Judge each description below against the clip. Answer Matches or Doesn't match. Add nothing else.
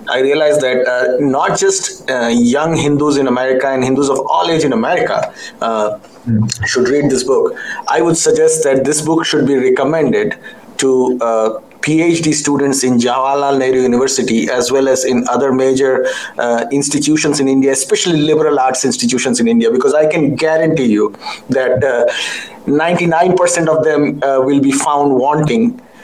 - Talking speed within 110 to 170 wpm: Matches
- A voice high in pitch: Doesn't match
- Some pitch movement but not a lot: Matches